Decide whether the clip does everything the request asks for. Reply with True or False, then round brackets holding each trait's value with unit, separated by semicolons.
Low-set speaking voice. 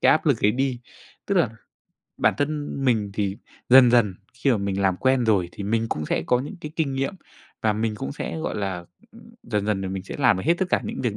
True (115 Hz)